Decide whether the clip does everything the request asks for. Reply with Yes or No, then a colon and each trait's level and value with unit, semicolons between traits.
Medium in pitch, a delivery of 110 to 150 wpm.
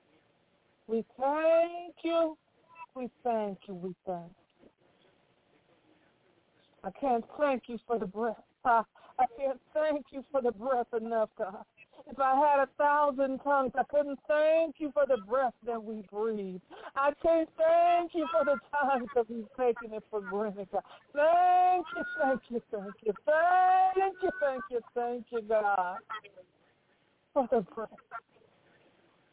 No: very high, 265 Hz; average, 145 wpm